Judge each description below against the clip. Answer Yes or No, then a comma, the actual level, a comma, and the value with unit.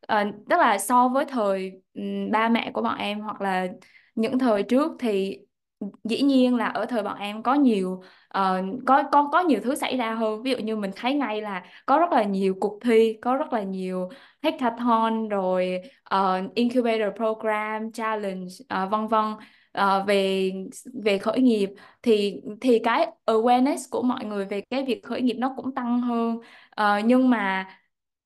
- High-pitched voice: Yes, high, 220 Hz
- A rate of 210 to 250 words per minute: No, average, 185 wpm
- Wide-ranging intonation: No, average, 3.6 semitones